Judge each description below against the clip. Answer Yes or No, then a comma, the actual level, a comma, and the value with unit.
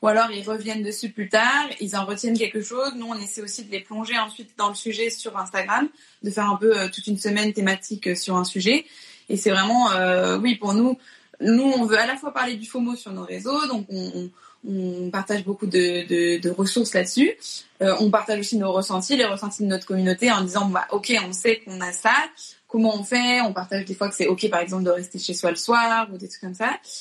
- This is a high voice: Yes, high, 210 Hz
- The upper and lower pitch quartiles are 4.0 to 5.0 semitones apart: No, average, 3.3 semitones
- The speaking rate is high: Yes, fast, 245 wpm